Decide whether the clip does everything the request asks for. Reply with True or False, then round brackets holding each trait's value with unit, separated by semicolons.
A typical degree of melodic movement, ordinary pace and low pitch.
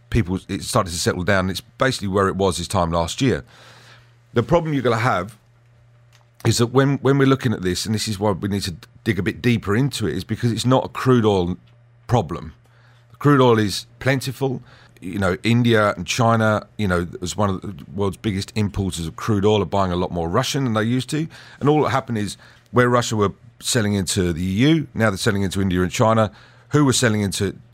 False (3.8 semitones; 225 wpm; 115 Hz)